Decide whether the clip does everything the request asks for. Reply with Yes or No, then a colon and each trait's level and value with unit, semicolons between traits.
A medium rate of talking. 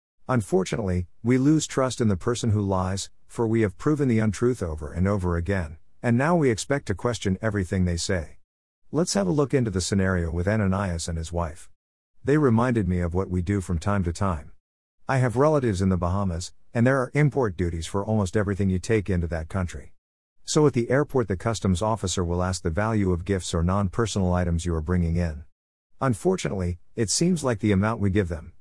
No: fast, 210 wpm